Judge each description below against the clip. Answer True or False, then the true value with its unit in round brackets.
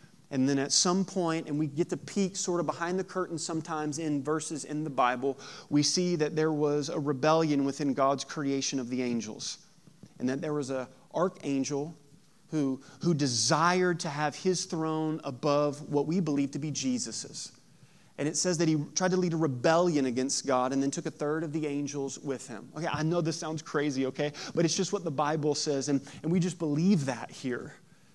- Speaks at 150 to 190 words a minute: False (205 wpm)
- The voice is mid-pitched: True (150 Hz)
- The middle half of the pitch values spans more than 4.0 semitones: False (3.1 semitones)